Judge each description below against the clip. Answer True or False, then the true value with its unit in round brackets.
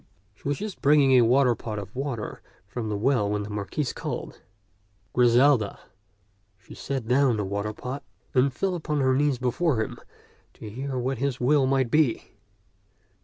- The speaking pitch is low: True (125 Hz)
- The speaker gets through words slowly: False (160 wpm)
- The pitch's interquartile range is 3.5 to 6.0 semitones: True (4.1 semitones)